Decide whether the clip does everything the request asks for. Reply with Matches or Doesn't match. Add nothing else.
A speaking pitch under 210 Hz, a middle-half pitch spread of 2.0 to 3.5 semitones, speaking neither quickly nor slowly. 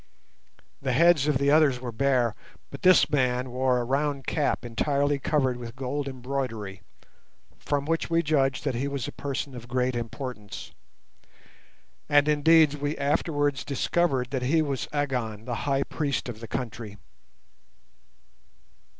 Matches